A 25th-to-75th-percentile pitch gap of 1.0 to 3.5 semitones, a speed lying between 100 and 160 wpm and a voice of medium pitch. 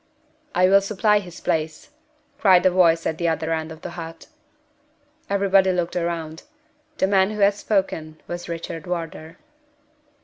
Yes: average, 2.9 semitones; average, 150 wpm; medium, 175 Hz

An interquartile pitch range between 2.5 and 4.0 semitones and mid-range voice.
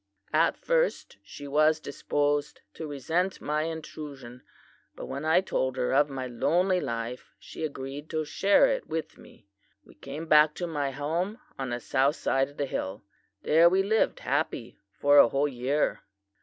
Yes: average, 3.1 semitones; medium, 145 Hz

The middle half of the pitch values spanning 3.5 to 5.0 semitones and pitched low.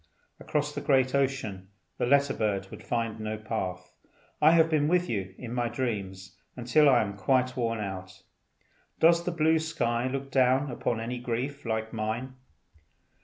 Yes: average, 4.2 semitones; low, 125 Hz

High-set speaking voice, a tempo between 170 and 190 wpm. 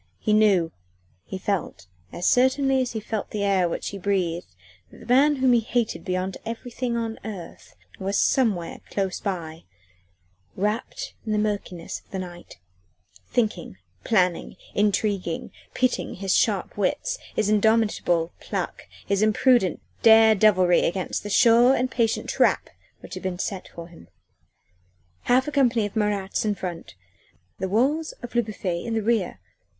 No: high, 210 Hz; average, 155 wpm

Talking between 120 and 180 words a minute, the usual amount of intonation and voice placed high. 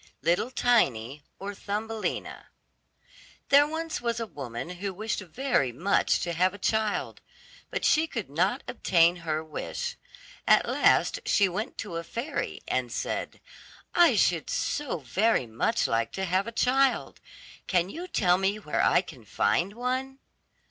No: average, 155 wpm; wide, 6.2 semitones; high, 200 Hz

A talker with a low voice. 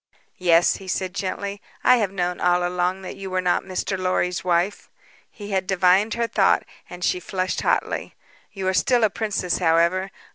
No: medium, 185 Hz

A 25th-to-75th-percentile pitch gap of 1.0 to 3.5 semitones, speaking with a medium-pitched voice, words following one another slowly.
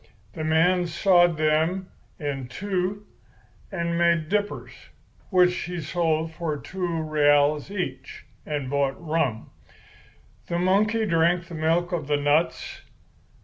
Yes: average, 2.7 semitones; medium, 170 Hz; slow, 120 wpm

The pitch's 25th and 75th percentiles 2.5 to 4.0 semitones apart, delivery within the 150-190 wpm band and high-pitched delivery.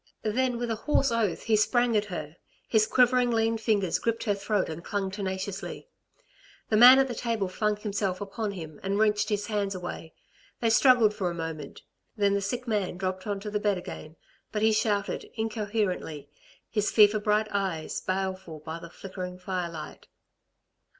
Yes: average, 3.0 semitones; average, 175 wpm; high, 205 Hz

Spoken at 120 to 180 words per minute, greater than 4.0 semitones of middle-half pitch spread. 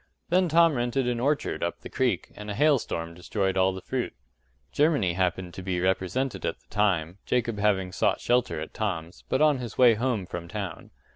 No: average, 195 wpm; wide, 5.5 semitones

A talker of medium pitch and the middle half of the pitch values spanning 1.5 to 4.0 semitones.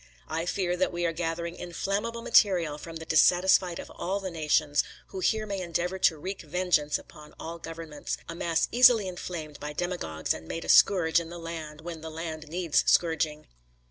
Yes: medium, 170 Hz; narrow, 2.4 semitones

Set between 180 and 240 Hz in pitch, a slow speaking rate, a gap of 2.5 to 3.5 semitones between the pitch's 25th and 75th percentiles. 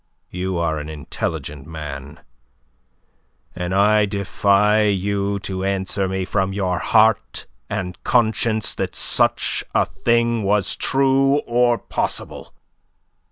No: low, 100 Hz; slow, 115 wpm; average, 3.2 semitones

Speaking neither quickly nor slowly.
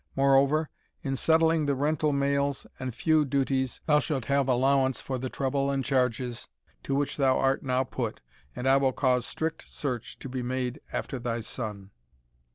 Yes: average, 170 wpm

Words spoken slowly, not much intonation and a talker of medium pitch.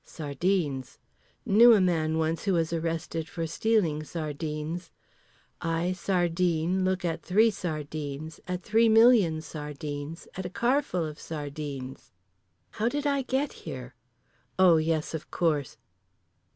No: slow, 125 wpm; average, 3.5 semitones; medium, 165 Hz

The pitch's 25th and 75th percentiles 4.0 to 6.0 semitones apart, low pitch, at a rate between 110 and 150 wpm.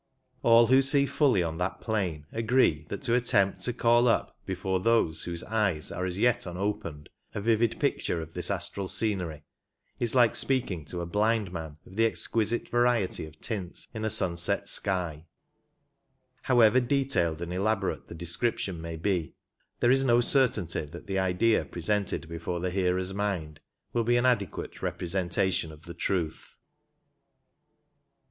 No: average, 5.2 semitones; very low, 95 Hz; average, 160 wpm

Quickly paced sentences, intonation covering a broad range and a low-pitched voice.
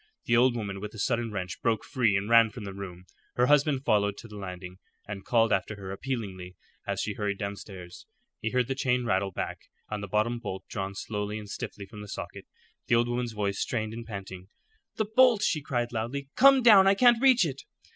No: fast, 215 wpm; average, 4.1 semitones; low, 110 Hz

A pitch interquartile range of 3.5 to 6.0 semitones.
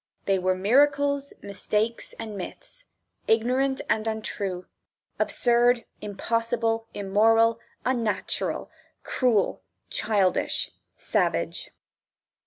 No: average, 3.1 semitones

